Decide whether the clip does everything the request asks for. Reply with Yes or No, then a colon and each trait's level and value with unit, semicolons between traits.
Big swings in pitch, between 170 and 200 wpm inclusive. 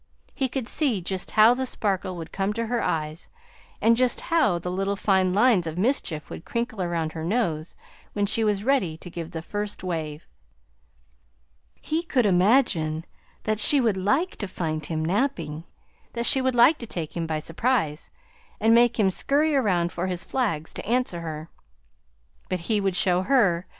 Yes: wide, 5.9 semitones; average, 180 wpm